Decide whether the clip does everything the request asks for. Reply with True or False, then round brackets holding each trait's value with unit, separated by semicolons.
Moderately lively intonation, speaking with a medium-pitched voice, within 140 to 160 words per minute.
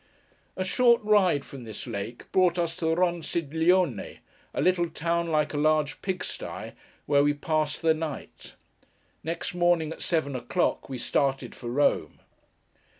True (3.3 semitones; 160 Hz; 150 wpm)